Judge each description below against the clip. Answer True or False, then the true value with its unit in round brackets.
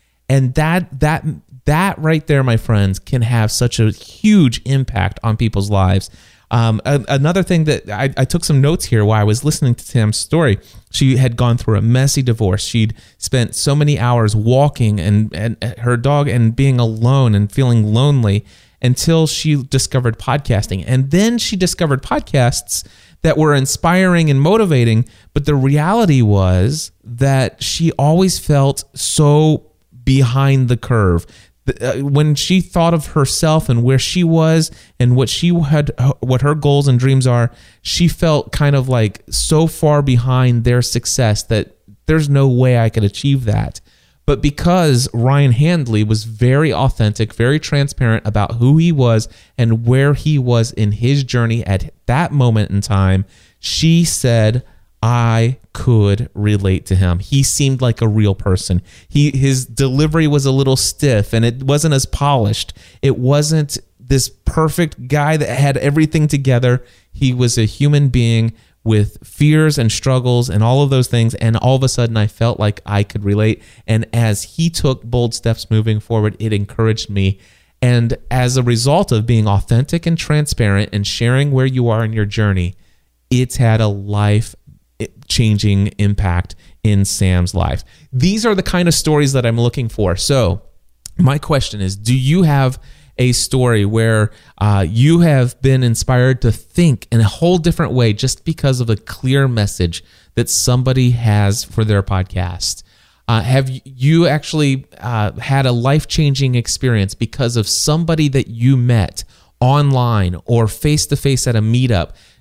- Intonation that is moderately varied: True (4.6 semitones)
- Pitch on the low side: True (125 Hz)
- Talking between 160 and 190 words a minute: True (165 wpm)